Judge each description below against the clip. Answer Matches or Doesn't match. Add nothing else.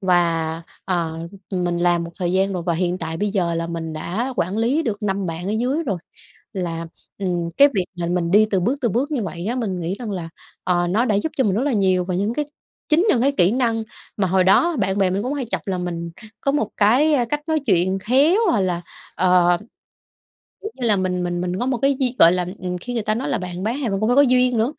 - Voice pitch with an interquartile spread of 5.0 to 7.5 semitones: Matches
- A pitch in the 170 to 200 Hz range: Matches